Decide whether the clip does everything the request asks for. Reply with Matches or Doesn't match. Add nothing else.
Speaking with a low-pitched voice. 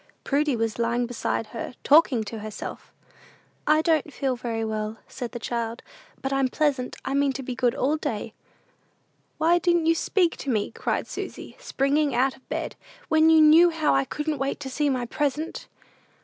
Doesn't match